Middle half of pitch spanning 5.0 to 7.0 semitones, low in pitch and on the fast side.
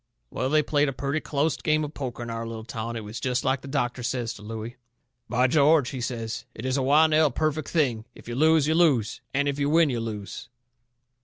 No: average, 4.2 semitones; low, 130 Hz; fast, 235 wpm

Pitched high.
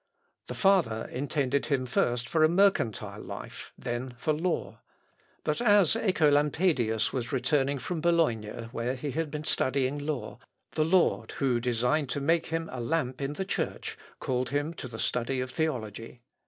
No: medium, 140 Hz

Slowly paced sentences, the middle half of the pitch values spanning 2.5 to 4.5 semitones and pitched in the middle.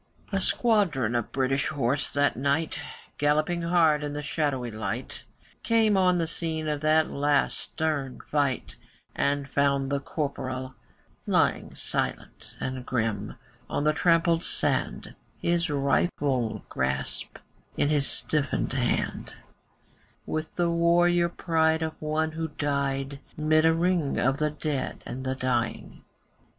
Yes: slow, 130 wpm; average, 3.2 semitones; medium, 150 Hz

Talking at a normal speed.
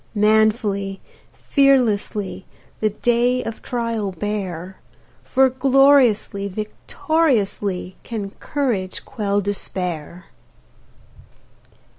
No: slow, 70 wpm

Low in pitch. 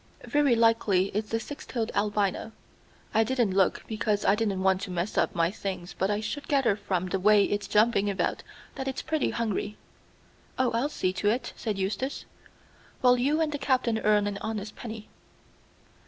No: high, 215 Hz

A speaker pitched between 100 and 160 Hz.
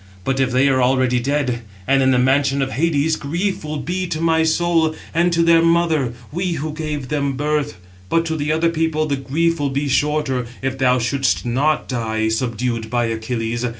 Yes: medium, 140 Hz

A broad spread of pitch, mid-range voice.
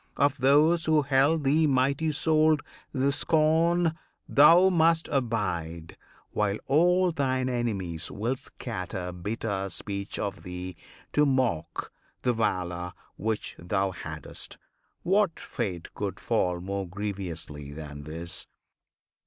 No: wide, 8.7 semitones; low, 115 Hz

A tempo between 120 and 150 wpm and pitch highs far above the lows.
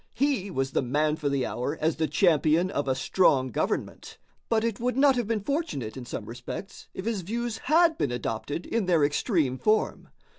No: average, 195 wpm; wide, 9.0 semitones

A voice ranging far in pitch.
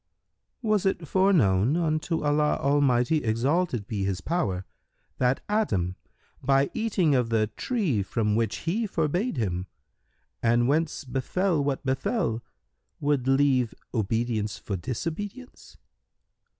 Yes: wide, 6.7 semitones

